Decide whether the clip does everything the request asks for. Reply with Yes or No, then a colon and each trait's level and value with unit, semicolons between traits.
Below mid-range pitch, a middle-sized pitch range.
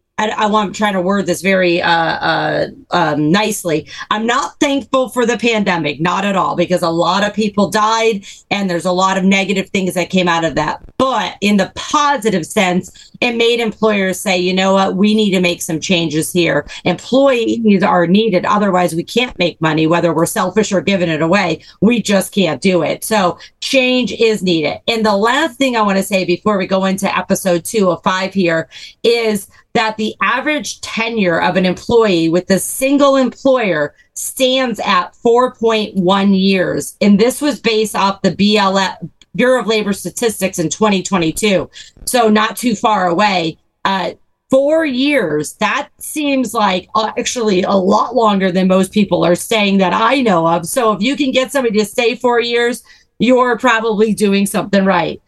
No: high, 200 Hz; average, 4.1 semitones